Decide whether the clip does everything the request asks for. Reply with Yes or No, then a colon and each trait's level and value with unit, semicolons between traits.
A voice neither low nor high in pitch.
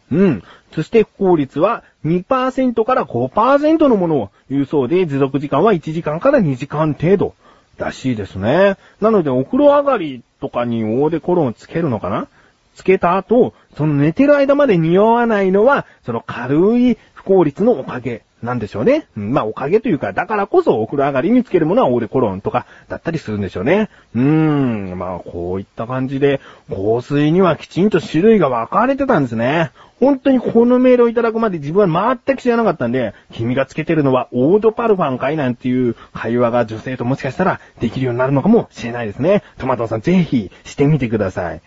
Yes: medium, 155 Hz